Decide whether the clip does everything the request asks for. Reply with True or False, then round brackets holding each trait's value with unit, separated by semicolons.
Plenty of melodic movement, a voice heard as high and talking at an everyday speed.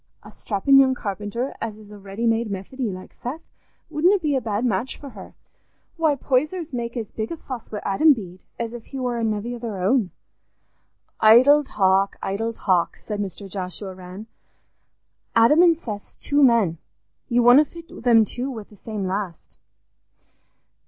False (4.6 semitones; 230 Hz; 170 wpm)